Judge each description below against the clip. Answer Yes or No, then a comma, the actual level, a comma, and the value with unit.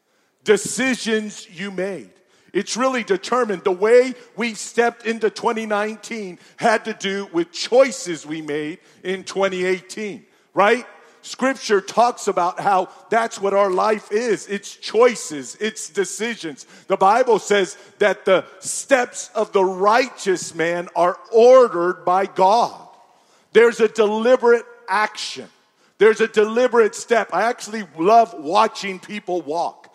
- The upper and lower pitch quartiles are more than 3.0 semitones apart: Yes, average, 3.8 semitones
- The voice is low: No, high, 210 Hz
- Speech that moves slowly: Yes, slow, 125 wpm